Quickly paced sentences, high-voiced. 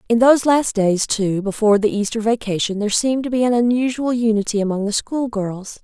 No: average, 195 wpm; high, 225 Hz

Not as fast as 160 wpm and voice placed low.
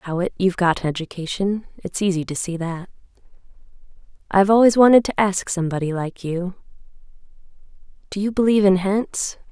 No: average, 140 wpm; high, 190 Hz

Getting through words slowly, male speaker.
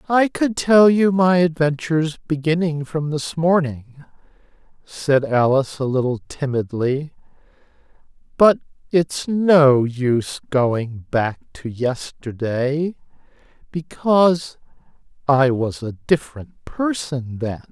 Yes: slow, 100 wpm; male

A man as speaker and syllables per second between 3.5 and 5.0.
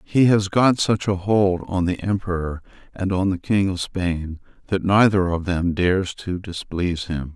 Yes: male; 4.4 syllables/s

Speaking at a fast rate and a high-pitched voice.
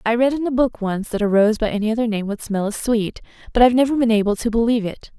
Yes: fast, 290 wpm; high, 225 Hz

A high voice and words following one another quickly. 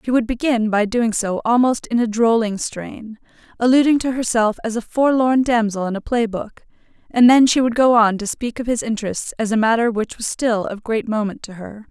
Yes: high, 230 Hz; fast, 220 wpm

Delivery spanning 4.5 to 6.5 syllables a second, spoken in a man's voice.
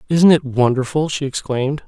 Yes: 5.5 syllables/s; male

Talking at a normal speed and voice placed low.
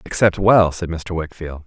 Yes: average, 180 wpm; very low, 85 Hz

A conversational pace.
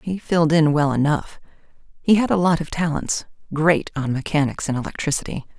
Yes: average, 150 wpm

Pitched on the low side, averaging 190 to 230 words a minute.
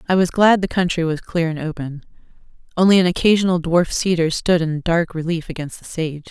No: medium, 170 Hz; average, 200 wpm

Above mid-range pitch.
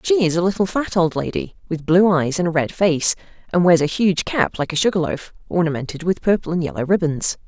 No: medium, 175 Hz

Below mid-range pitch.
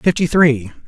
No: medium, 145 Hz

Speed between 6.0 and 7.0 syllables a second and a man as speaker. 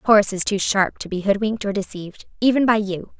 No: 6.3 syllables/s; female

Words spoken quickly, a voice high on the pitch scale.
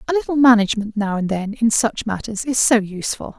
Yes: fast, 215 wpm; high, 225 Hz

